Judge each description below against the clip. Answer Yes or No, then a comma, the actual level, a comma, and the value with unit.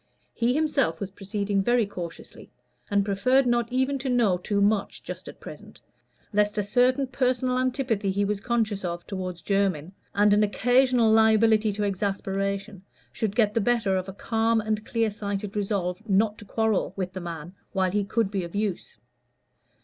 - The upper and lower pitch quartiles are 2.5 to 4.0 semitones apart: Yes, average, 2.9 semitones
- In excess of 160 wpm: Yes, average, 170 wpm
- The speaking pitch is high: Yes, high, 210 Hz